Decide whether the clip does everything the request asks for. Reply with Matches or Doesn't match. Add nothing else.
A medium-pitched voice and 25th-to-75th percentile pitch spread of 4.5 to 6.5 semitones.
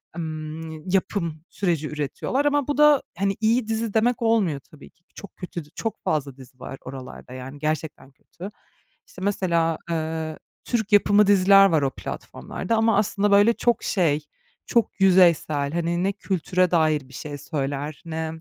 Matches